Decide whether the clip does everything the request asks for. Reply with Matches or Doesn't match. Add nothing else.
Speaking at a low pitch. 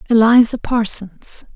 Doesn't match